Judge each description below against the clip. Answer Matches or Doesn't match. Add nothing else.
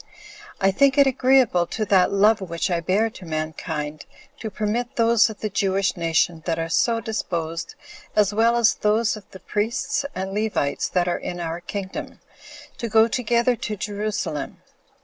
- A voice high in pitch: Matches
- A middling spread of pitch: Matches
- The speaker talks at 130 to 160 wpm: Doesn't match